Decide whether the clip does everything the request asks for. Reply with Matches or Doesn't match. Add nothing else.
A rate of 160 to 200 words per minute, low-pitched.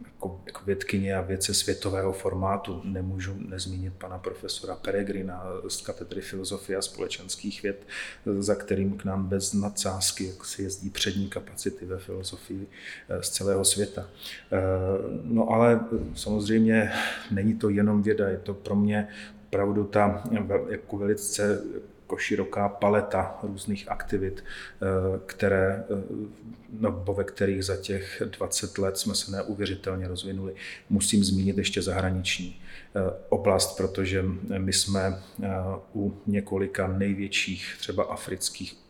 Doesn't match